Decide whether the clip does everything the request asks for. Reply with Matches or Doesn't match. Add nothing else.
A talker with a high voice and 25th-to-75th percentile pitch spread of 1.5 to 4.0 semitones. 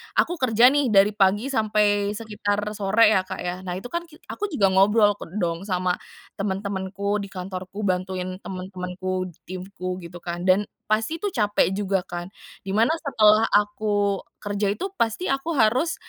Matches